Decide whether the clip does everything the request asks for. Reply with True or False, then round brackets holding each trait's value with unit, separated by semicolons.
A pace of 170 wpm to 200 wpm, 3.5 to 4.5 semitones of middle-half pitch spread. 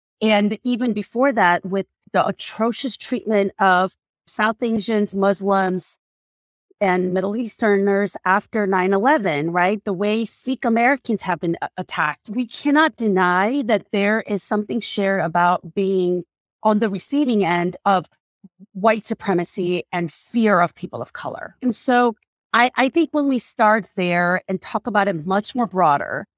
False (150 wpm; 3.8 semitones)